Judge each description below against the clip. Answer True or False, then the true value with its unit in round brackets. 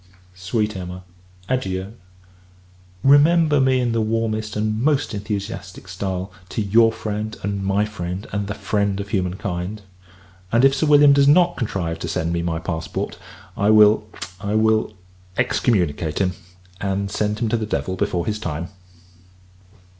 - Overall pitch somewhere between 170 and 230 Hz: False (105 Hz)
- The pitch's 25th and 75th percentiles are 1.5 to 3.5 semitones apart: True (3.1 semitones)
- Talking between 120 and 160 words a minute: True (150 wpm)